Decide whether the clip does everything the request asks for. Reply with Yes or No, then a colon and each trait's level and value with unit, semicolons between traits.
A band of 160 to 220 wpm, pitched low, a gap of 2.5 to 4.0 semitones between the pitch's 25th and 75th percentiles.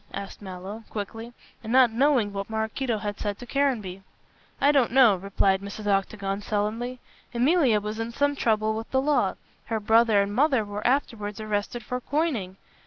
No: average, 170 wpm; high, 220 Hz; average, 3.5 semitones